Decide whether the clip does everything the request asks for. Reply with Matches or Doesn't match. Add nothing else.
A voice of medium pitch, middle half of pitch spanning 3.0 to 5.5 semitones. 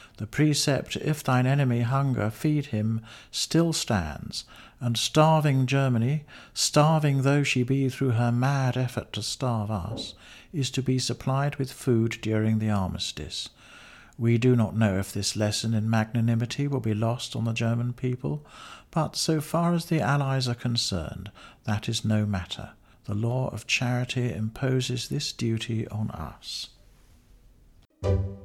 Doesn't match